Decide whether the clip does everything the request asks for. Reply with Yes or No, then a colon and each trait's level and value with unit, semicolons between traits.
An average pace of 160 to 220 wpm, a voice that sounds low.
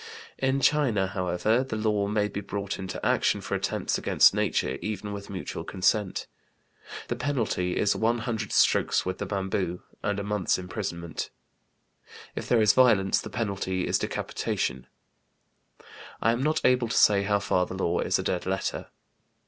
Yes: average, 165 wpm; low, 100 Hz